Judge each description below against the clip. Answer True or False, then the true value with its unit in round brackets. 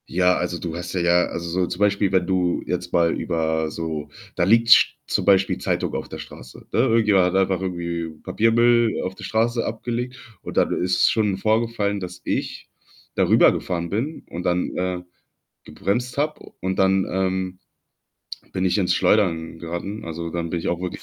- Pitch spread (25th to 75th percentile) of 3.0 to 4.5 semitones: True (3.3 semitones)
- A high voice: False (95 Hz)